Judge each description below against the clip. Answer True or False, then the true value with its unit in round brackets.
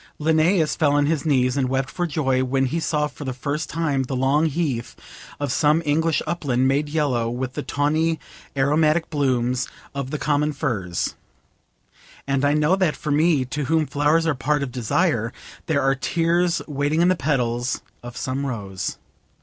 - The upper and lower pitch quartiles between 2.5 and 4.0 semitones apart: True (3.2 semitones)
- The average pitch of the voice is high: False (145 Hz)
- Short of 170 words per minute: False (175 wpm)